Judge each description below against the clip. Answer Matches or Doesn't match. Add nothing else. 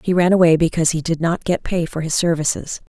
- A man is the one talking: Doesn't match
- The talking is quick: Matches